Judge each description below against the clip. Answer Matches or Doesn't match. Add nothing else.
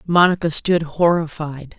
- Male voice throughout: Doesn't match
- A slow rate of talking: Matches